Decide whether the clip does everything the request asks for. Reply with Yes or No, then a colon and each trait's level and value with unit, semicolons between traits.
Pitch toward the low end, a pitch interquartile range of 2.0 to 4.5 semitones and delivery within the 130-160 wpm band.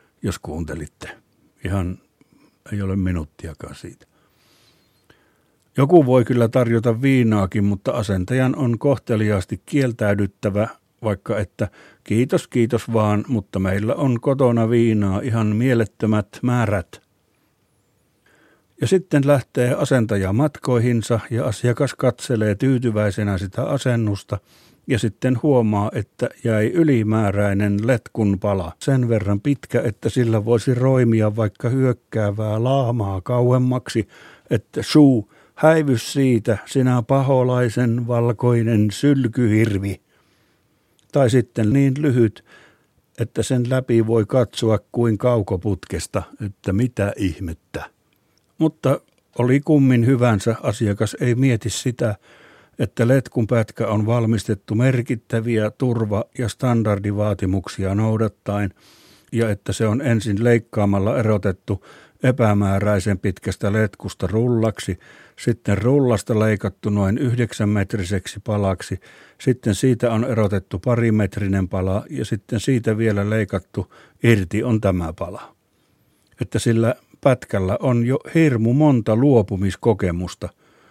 No: low, 115 Hz; average, 3.4 semitones; average, 105 wpm